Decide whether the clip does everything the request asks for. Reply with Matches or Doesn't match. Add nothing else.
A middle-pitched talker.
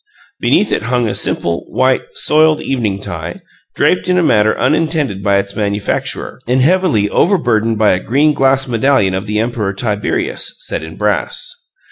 Doesn't match